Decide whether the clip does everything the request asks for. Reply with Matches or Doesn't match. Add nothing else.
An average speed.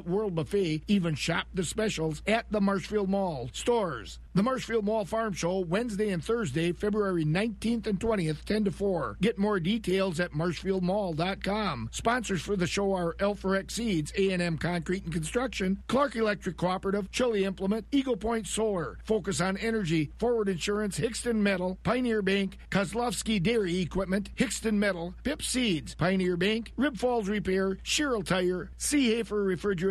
Matches